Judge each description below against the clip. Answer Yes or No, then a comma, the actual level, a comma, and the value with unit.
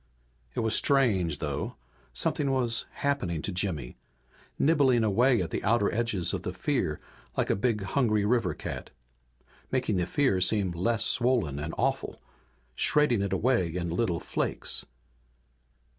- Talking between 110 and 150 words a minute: Yes, average, 145 wpm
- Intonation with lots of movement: Yes, wide, 5.8 semitones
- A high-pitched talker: No, low, 105 Hz